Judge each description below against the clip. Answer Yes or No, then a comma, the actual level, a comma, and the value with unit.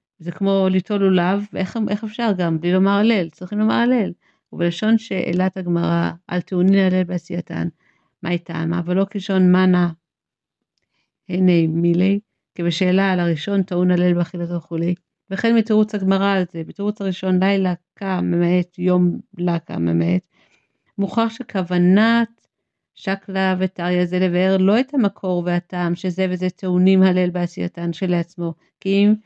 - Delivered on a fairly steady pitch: Yes, narrow, 2.0 semitones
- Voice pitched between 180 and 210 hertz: Yes, medium, 185 Hz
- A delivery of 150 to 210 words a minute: No, slow, 135 wpm